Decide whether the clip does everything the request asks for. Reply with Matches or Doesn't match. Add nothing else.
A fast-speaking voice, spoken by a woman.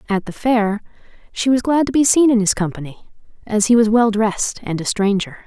Matches